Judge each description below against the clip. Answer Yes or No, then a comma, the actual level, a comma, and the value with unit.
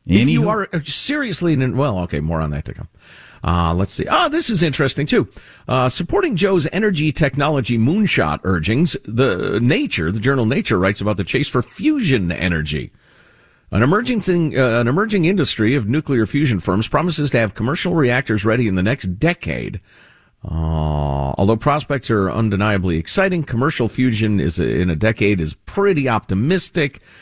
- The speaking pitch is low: Yes, low, 125 Hz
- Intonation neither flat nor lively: No, wide, 8.2 semitones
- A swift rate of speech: No, average, 165 wpm